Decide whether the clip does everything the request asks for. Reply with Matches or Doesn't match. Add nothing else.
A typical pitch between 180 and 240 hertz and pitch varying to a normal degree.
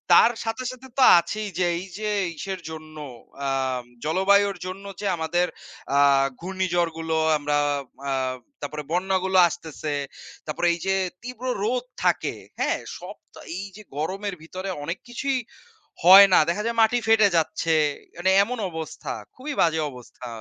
Matches